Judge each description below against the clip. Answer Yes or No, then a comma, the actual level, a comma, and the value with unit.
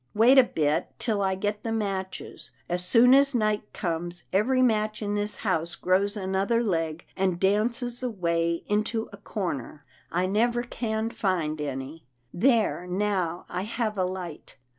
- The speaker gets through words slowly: No, average, 155 wpm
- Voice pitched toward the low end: No, high, 200 Hz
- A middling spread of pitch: Yes, average, 4.0 semitones